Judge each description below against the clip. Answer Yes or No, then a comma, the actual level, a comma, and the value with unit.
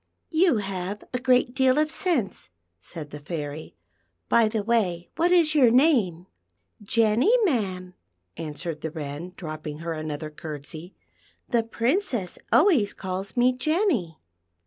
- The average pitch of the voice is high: Yes, high, 195 Hz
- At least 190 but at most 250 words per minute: No, average, 155 wpm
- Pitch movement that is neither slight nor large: No, wide, 8.0 semitones